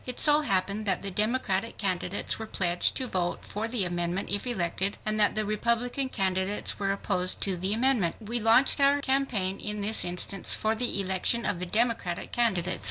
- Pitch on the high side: Yes, high, 205 Hz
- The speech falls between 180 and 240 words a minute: Yes, average, 185 wpm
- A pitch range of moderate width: Yes, average, 3.9 semitones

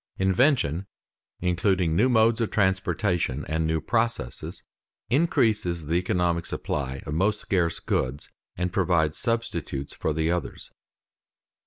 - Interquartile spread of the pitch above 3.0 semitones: Yes, average, 4.8 semitones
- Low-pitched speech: Yes, very low, 90 Hz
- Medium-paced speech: No, slow, 120 wpm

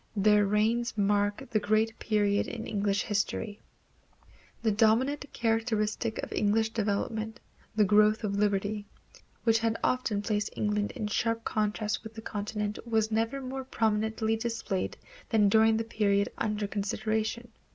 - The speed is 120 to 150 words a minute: Yes, average, 140 wpm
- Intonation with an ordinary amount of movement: No, narrow, 1.4 semitones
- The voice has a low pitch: No, high, 215 Hz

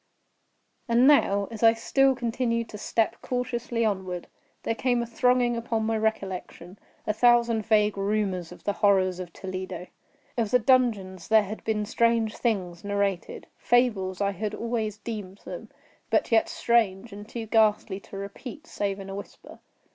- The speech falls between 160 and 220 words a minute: No, average, 150 wpm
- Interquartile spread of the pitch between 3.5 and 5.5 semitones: No, average, 3.0 semitones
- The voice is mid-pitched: No, high, 215 Hz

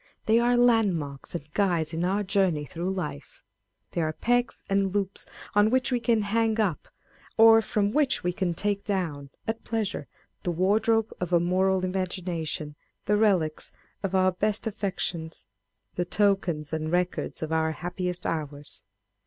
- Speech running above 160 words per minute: No, average, 155 wpm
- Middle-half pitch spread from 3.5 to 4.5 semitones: Yes, average, 4.1 semitones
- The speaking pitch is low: No, medium, 185 Hz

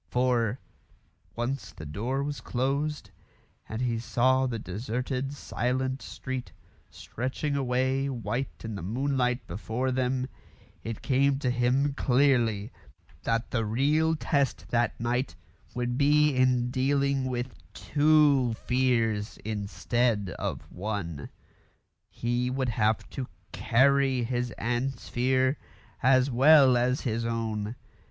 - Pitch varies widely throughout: No, average, 2.7 semitones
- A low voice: Yes, low, 125 Hz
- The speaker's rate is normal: No, slow, 115 wpm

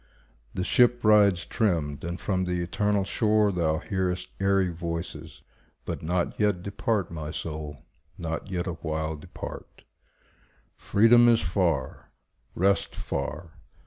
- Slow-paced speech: Yes, slow, 120 wpm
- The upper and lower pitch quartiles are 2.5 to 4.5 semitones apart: Yes, average, 3.7 semitones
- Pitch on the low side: Yes, very low, 90 Hz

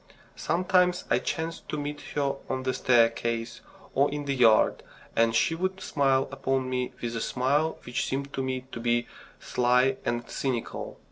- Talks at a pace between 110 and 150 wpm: No, average, 165 wpm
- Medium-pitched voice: No, low, 130 Hz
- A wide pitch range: No, average, 3.3 semitones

